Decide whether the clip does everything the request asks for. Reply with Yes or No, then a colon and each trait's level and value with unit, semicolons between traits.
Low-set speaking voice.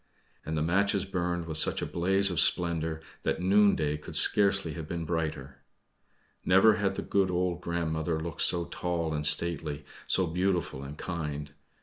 Yes: very low, 85 Hz